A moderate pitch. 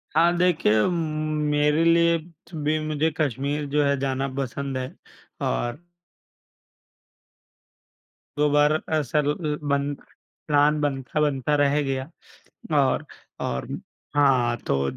Yes: medium, 145 Hz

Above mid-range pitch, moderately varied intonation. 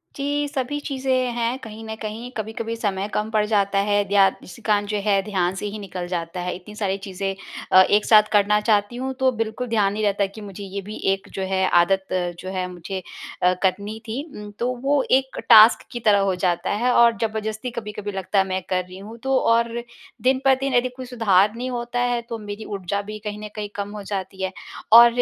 Yes: high, 210 Hz; average, 3.3 semitones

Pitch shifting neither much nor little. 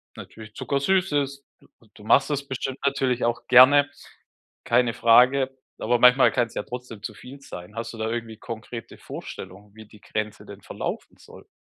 Yes: average, 3.5 semitones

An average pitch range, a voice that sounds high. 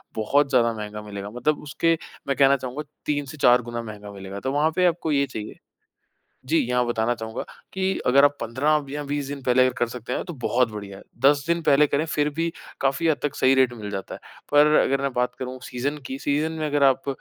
No: average, 3.6 semitones; low, 135 Hz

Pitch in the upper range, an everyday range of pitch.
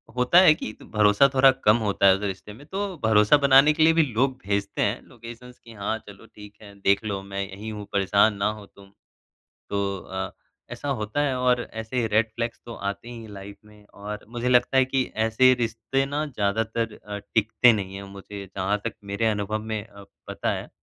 No: low, 110 Hz; average, 3.5 semitones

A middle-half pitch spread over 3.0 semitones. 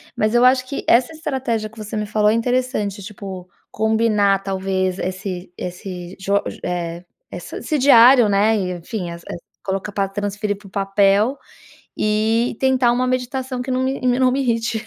Yes: average, 4.2 semitones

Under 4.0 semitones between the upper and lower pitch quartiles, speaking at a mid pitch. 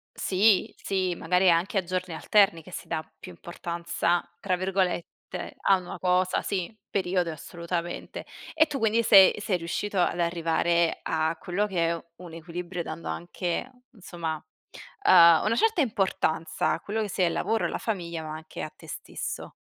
Yes: narrow, 2.6 semitones; medium, 180 Hz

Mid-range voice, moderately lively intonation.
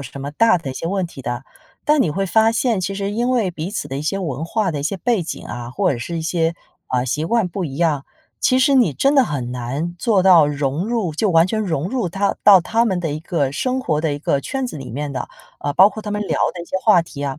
No: medium, 170 Hz; wide, 6.4 semitones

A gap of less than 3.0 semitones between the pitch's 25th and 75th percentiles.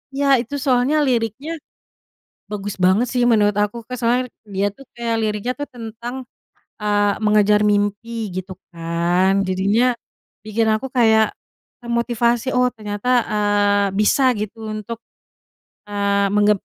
Yes: narrow, 2.6 semitones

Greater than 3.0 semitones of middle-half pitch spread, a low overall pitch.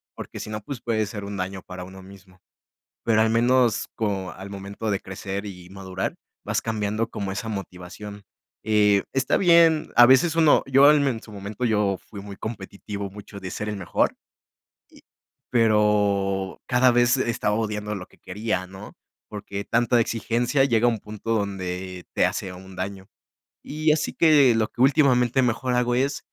Yes: average, 3.7 semitones; low, 105 Hz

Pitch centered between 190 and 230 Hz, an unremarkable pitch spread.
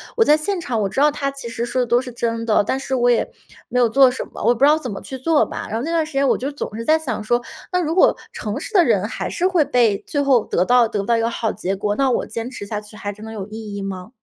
No: high, 240 Hz; average, 4.3 semitones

